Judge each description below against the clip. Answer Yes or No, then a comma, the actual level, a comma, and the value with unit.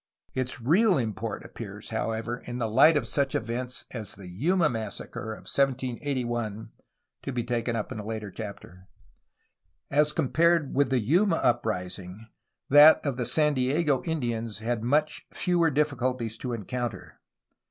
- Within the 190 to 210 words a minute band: No, average, 145 wpm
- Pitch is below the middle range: Yes, low, 125 Hz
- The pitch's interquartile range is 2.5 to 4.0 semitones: No, average, 4.6 semitones